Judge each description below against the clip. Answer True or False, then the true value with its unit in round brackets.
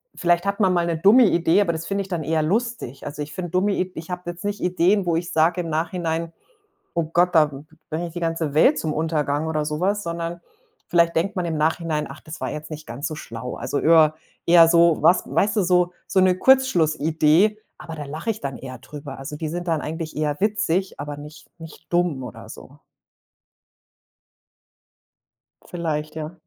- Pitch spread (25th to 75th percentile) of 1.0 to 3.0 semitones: True (2.7 semitones)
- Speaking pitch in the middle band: True (165 Hz)